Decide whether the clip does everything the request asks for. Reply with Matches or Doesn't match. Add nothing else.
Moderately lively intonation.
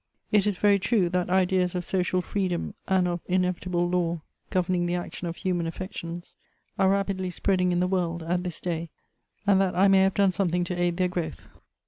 Doesn't match